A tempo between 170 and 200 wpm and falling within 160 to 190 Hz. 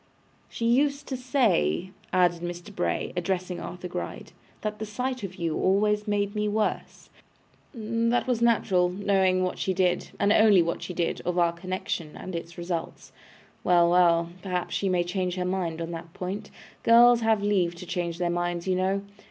Yes: average, 175 wpm; medium, 185 Hz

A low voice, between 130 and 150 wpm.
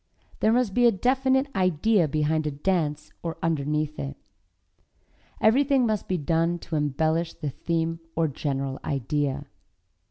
No: medium, 160 Hz; slow, 135 wpm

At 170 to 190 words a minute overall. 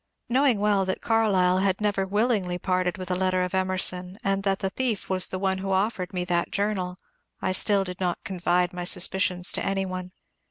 No: average, 200 wpm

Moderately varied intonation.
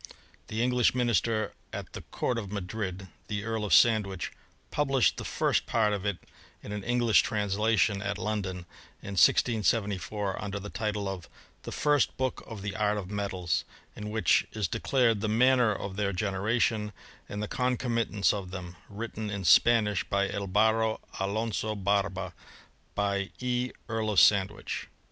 No: narrow, 2.2 semitones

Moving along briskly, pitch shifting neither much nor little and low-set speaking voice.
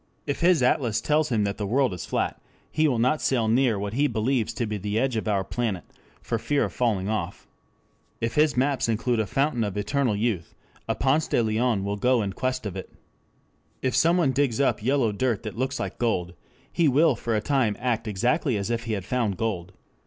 Yes: fast, 215 wpm; average, 4.0 semitones; low, 115 Hz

